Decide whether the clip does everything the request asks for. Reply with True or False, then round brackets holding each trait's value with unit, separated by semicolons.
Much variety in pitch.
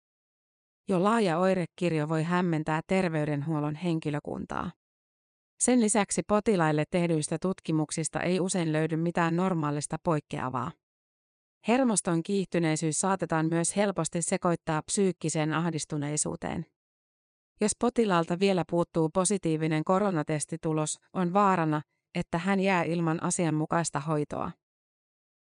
False (3.0 semitones)